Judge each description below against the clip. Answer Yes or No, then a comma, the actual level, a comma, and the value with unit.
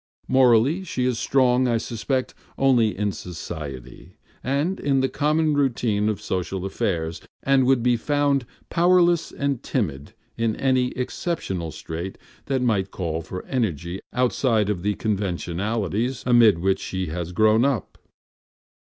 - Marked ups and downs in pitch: Yes, wide, 5.9 semitones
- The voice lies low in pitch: Yes, low, 115 Hz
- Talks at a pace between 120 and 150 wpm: Yes, slow, 135 wpm